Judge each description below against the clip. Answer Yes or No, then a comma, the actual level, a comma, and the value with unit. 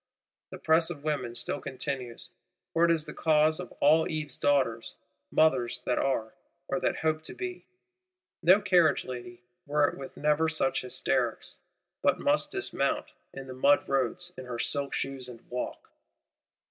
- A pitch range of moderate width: Yes, average, 3.9 semitones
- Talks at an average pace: Yes, average, 160 wpm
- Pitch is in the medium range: Yes, medium, 145 Hz